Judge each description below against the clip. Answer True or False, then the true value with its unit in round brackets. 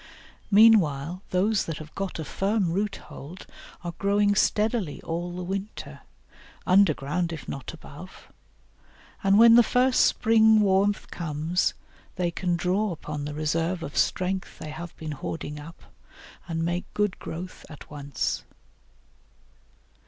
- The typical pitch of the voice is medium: True (180 Hz)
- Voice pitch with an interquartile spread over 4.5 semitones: False (4.2 semitones)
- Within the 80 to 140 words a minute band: True (135 wpm)